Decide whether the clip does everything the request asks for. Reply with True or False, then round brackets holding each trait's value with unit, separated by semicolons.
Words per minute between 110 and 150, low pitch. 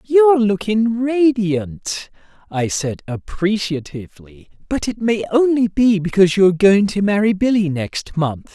False (135 wpm; 200 Hz)